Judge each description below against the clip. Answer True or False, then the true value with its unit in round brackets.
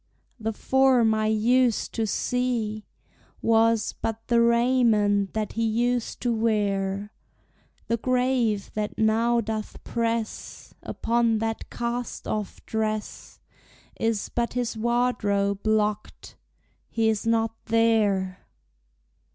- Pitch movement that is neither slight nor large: False (1.7 semitones)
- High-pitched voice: True (225 Hz)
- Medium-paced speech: False (110 wpm)